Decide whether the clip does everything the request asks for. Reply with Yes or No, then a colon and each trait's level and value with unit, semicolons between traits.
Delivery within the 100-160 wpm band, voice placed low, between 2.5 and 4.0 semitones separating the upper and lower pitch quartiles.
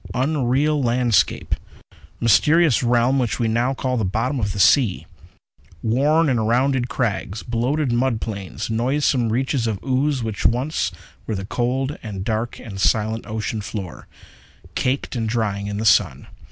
Yes: average, 150 wpm; low, 120 Hz; average, 3.2 semitones